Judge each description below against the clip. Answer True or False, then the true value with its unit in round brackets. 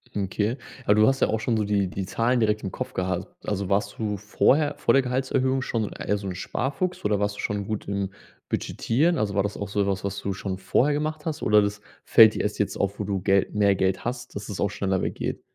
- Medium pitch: False (105 Hz)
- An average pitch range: True (3.3 semitones)